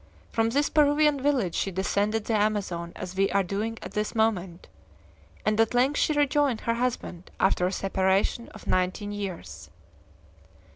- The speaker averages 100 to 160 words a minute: Yes, average, 155 wpm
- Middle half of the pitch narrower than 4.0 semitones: No, average, 4.3 semitones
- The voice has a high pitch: Yes, high, 210 Hz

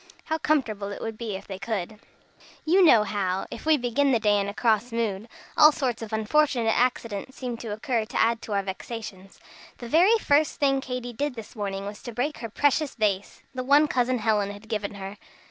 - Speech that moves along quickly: Yes, fast, 210 wpm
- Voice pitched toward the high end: Yes, high, 230 Hz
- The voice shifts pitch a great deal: No, average, 4.2 semitones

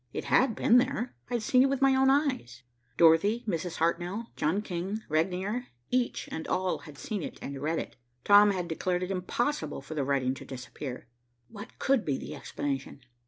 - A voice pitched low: No, medium, 185 Hz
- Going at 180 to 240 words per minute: Yes, average, 190 wpm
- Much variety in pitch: Yes, wide, 7.2 semitones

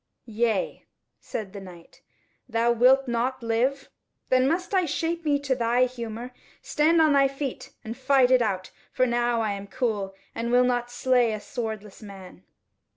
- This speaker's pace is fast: No, average, 165 wpm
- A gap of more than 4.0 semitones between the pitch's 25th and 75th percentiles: No, average, 3.3 semitones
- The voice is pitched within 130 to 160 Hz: No, high, 240 Hz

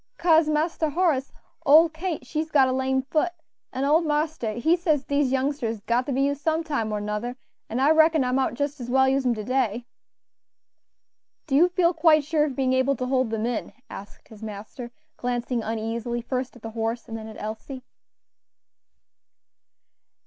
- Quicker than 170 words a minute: Yes, average, 185 wpm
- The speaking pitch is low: No, very high, 265 Hz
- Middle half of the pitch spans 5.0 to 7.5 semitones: No, average, 4.5 semitones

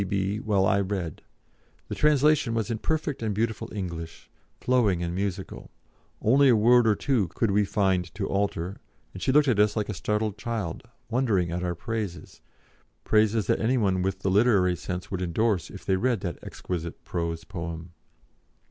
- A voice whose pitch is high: No, low, 100 Hz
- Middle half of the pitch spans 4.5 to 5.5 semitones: No, average, 3.8 semitones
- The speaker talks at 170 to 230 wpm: Yes, average, 175 wpm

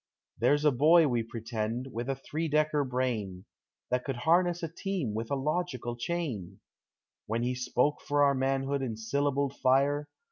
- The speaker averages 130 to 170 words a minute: Yes, average, 165 wpm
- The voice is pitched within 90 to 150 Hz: Yes, low, 135 Hz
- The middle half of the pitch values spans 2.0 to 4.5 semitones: Yes, average, 3.8 semitones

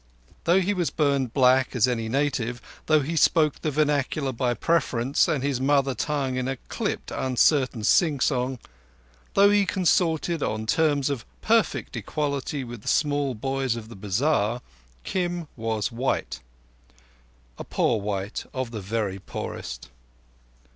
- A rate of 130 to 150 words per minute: Yes, average, 140 wpm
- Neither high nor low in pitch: No, low, 130 Hz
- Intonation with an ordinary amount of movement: Yes, average, 4.8 semitones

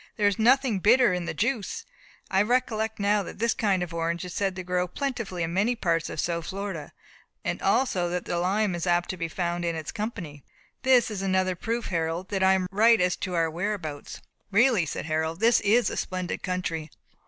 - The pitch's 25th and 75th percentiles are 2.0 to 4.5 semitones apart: Yes, average, 3.9 semitones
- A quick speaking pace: Yes, fast, 210 wpm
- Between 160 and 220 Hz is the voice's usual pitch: Yes, medium, 185 Hz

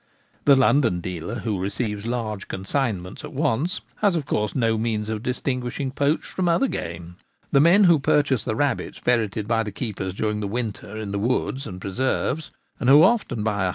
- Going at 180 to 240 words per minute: Yes, average, 190 wpm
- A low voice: Yes, low, 115 Hz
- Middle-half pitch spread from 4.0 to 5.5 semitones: Yes, average, 5.0 semitones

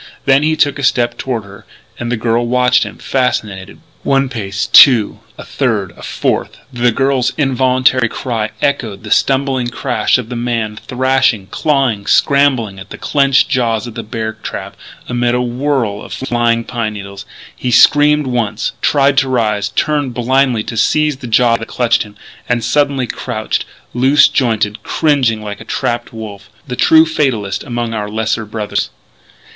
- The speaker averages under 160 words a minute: No, average, 165 wpm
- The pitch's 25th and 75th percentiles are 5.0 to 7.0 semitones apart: No, average, 3.3 semitones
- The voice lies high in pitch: No, low, 120 Hz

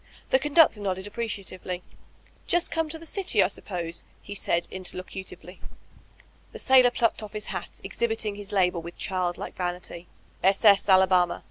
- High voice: Yes, high, 195 Hz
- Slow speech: No, average, 155 wpm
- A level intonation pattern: No, average, 4.1 semitones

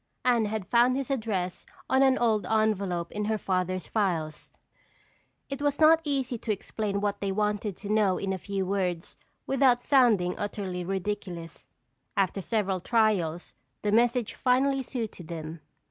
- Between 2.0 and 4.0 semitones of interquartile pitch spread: No, average, 4.6 semitones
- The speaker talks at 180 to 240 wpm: No, average, 150 wpm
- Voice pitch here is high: Yes, high, 210 Hz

